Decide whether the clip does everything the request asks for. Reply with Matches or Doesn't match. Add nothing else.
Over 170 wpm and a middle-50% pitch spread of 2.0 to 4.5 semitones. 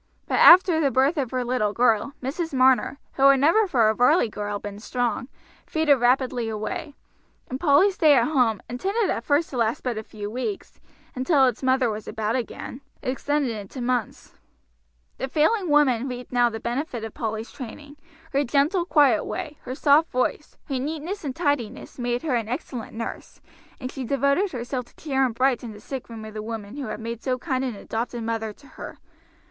Matches